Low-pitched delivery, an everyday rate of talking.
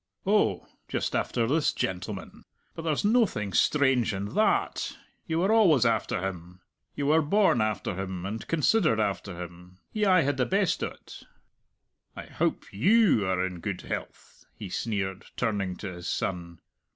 Yes: low, 110 Hz; average, 160 wpm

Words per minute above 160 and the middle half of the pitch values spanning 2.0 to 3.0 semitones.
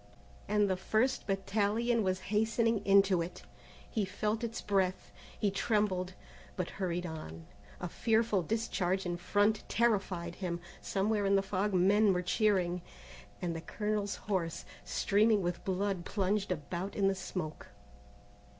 No: average, 140 wpm; narrow, 2.6 semitones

